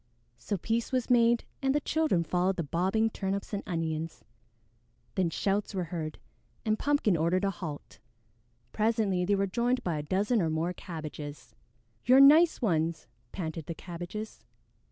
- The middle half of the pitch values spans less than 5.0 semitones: No, average, 5.3 semitones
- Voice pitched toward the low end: No, high, 190 Hz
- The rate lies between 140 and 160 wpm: Yes, average, 155 wpm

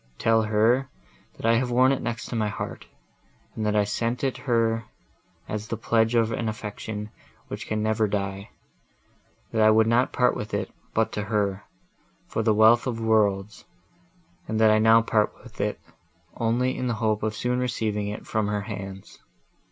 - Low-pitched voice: Yes, low, 110 Hz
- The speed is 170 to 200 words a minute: Yes, average, 180 wpm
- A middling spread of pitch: No, narrow, 1.6 semitones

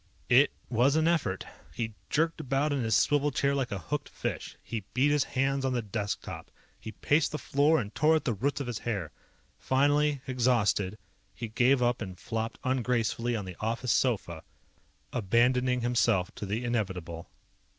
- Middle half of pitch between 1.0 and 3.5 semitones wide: No, average, 4.1 semitones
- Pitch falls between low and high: No, low, 120 Hz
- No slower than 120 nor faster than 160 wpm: No, average, 175 wpm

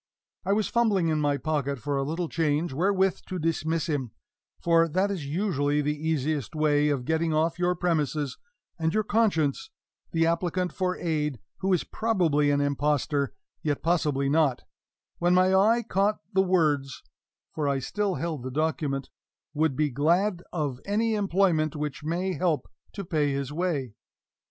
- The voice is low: No, medium, 160 Hz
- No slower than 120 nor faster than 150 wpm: No, average, 160 wpm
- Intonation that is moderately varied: Yes, average, 3.9 semitones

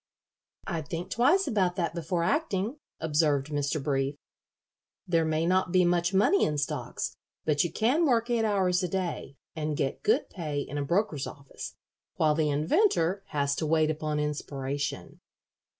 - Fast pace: No, average, 160 wpm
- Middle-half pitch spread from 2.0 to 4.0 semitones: No, average, 4.4 semitones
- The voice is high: No, medium, 165 Hz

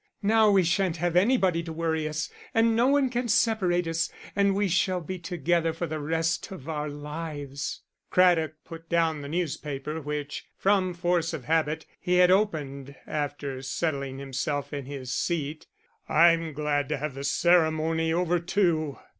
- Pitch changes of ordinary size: Yes, average, 3.3 semitones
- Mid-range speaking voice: Yes, medium, 165 Hz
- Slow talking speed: No, average, 165 wpm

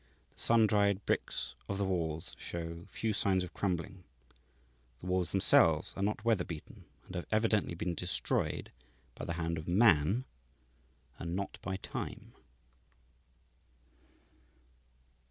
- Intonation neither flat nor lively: Yes, average, 3.2 semitones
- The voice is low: Yes, very low, 95 Hz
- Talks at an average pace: No, slow, 130 wpm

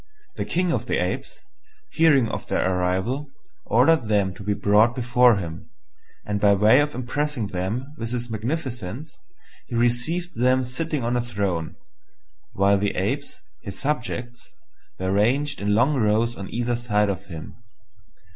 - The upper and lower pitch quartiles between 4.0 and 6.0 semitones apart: Yes, average, 4.4 semitones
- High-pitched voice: No, low, 120 Hz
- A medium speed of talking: Yes, average, 155 wpm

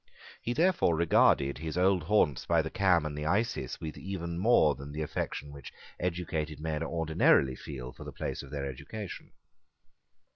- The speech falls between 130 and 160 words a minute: No, average, 170 wpm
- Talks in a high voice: No, very low, 80 Hz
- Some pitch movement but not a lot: Yes, average, 3.7 semitones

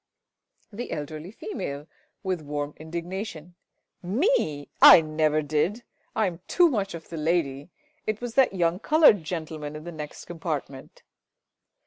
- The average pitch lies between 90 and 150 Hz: No, medium, 165 Hz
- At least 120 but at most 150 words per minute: Yes, slow, 135 wpm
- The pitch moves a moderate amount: Yes, average, 4.5 semitones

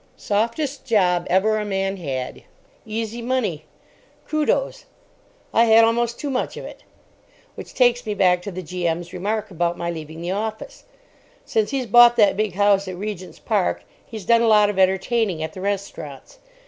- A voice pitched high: Yes, high, 205 Hz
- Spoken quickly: No, average, 165 wpm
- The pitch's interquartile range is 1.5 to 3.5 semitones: No, average, 4.1 semitones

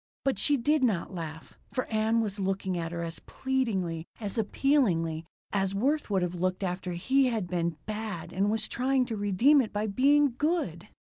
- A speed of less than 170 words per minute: No, average, 185 wpm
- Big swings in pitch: Yes, wide, 6.2 semitones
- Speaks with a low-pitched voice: No, high, 205 Hz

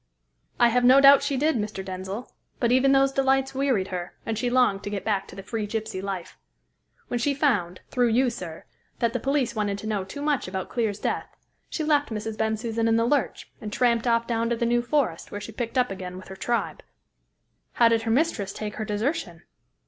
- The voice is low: No, high, 230 Hz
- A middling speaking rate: No, fast, 215 wpm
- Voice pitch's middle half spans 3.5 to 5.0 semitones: Yes, average, 3.8 semitones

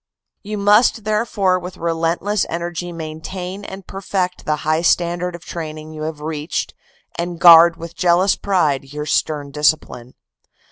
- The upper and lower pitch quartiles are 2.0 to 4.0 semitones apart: Yes, average, 2.9 semitones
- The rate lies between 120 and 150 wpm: Yes, average, 140 wpm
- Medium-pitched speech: Yes, medium, 170 Hz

